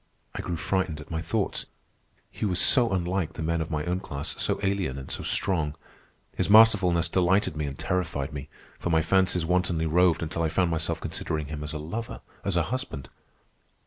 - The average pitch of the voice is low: Yes, very low, 85 Hz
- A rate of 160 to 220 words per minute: Yes, average, 195 wpm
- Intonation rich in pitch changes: No, average, 3.2 semitones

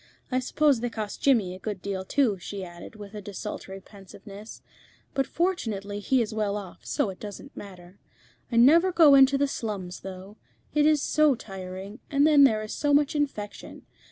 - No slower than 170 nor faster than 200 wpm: Yes, average, 185 wpm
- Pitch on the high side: Yes, high, 215 Hz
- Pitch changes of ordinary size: No, wide, 6.0 semitones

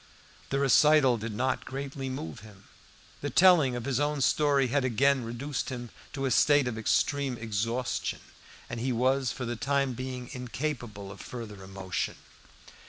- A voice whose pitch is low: Yes, low, 130 Hz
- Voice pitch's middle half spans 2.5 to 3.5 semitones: Yes, average, 3.2 semitones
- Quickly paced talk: No, average, 160 wpm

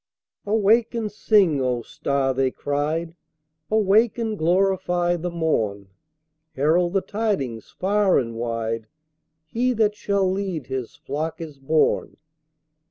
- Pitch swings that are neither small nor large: No, wide, 7.0 semitones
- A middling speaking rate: No, slow, 120 wpm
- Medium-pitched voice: Yes, medium, 170 Hz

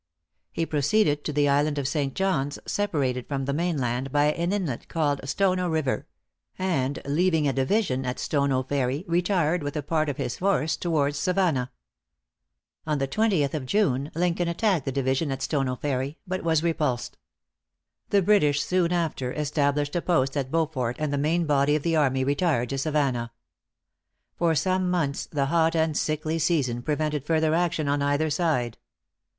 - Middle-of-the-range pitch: Yes, medium, 150 Hz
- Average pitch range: Yes, average, 3.6 semitones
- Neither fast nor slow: Yes, average, 165 wpm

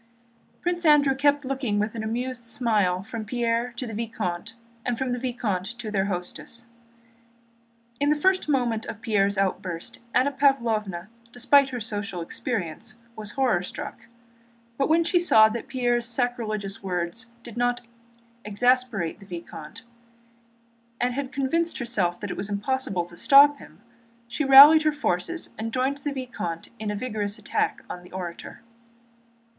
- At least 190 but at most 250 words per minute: No, average, 150 wpm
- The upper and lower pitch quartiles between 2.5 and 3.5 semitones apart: No, average, 4.6 semitones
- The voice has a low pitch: No, high, 235 Hz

